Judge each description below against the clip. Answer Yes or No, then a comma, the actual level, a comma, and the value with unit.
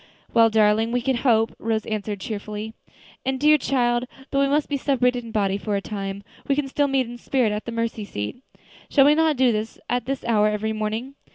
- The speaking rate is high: Yes, fast, 215 wpm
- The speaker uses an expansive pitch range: No, average, 3.8 semitones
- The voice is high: Yes, high, 230 Hz